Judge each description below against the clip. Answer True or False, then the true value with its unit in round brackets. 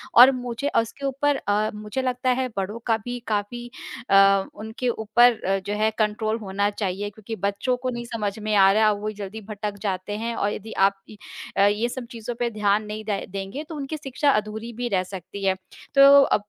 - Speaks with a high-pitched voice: True (215 Hz)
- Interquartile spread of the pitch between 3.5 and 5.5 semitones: False (3.0 semitones)